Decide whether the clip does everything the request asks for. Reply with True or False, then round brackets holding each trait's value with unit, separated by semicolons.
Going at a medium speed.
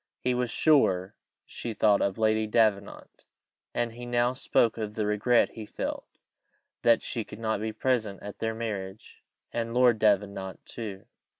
True (160 wpm)